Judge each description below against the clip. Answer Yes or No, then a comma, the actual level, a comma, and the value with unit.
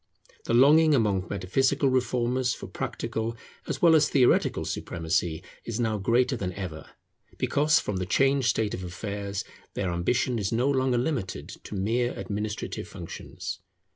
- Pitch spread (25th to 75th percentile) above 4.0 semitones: Yes, average, 5.0 semitones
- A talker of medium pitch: No, low, 115 Hz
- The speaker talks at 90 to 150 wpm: Yes, average, 145 wpm